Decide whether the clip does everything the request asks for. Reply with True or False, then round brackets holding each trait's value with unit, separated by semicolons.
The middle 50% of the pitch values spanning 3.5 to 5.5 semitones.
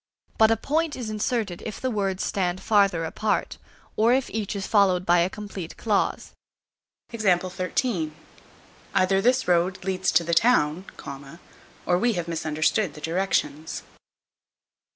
True (3.8 semitones)